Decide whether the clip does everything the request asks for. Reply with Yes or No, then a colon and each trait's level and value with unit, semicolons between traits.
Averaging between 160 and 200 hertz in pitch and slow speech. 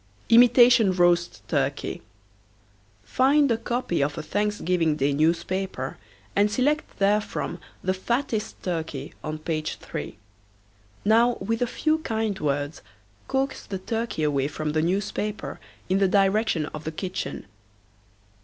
Yes: high, 190 Hz; slow, 125 wpm